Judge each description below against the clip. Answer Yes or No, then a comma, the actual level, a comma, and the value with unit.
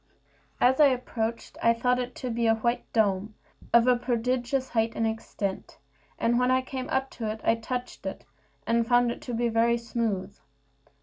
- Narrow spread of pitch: Yes, narrow, 1.8 semitones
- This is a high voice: Yes, high, 235 Hz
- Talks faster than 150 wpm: Yes, average, 185 wpm